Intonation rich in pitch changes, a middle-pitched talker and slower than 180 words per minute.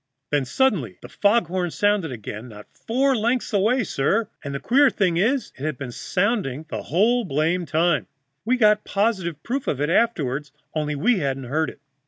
No: wide, 7.8 semitones; medium, 180 Hz; average, 185 wpm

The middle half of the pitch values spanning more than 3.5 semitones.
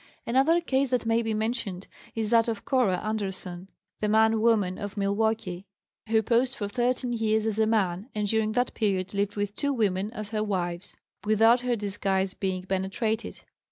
No: average, 2.7 semitones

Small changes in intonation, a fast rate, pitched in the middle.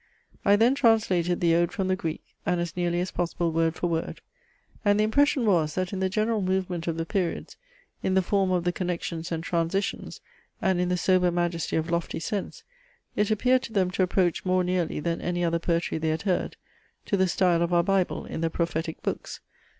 Yes: narrow, 2.2 semitones; fast, 210 wpm; medium, 180 Hz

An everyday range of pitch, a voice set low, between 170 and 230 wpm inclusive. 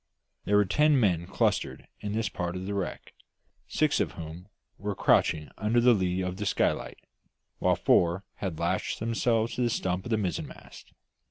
Yes: average, 3.9 semitones; low, 100 Hz; average, 175 wpm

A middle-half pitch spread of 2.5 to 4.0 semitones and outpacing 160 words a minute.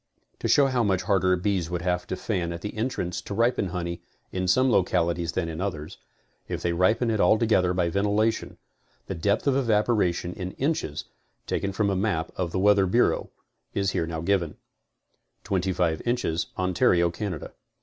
Yes: average, 3.5 semitones; average, 170 wpm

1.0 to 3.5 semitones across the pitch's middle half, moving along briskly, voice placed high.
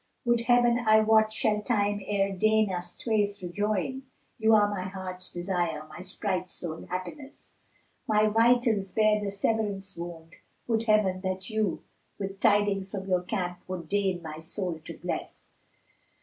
No: average, 2.9 semitones; average, 160 wpm; high, 200 Hz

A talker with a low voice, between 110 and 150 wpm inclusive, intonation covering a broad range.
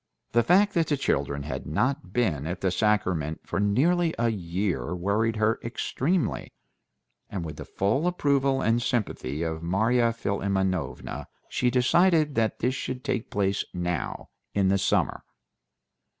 Yes: low, 105 Hz; average, 145 wpm; wide, 6.4 semitones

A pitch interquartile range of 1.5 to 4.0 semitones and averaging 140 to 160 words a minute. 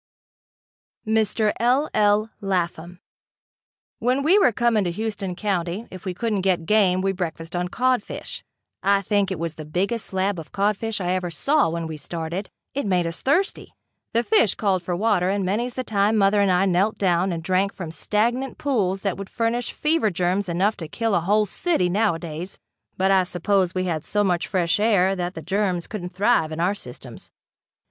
No: average, 3.4 semitones; average, 185 wpm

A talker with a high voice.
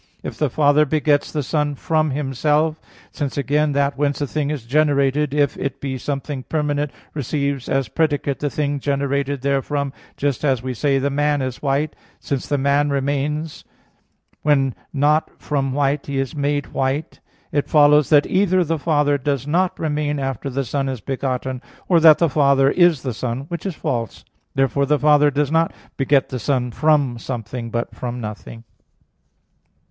No: medium, 140 Hz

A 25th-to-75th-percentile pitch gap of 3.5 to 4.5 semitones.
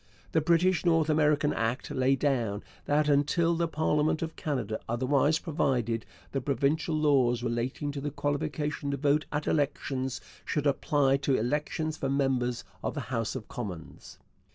No: average, 2.9 semitones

